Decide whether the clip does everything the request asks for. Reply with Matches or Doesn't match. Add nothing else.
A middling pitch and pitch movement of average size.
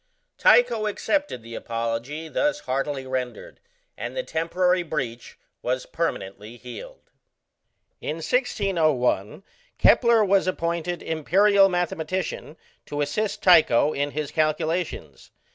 Doesn't match